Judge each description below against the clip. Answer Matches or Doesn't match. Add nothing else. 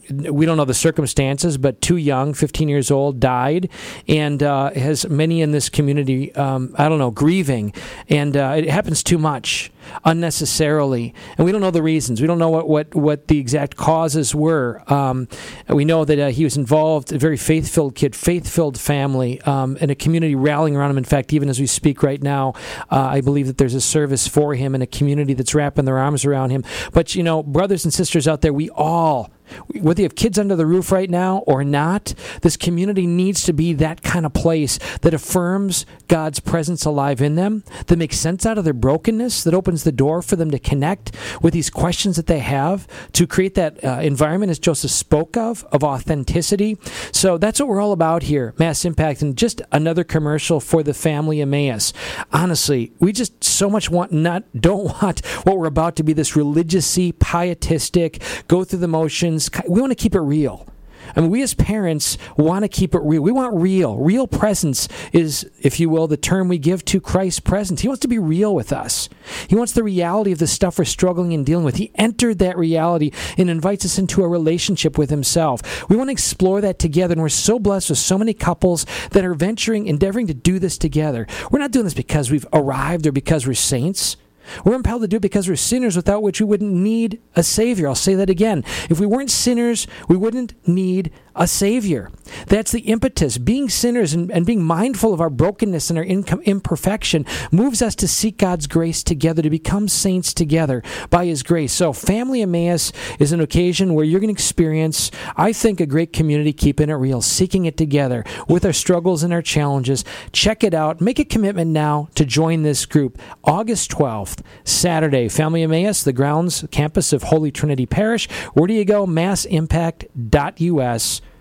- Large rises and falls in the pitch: Doesn't match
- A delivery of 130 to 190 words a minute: Doesn't match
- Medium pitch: Matches